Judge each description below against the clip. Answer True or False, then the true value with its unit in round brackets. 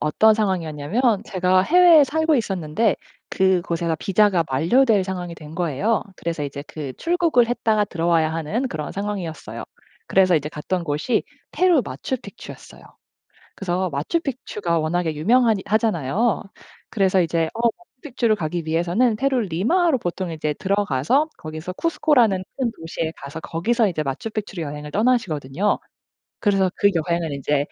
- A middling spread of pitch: False (6.1 semitones)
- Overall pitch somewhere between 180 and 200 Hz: True (185 Hz)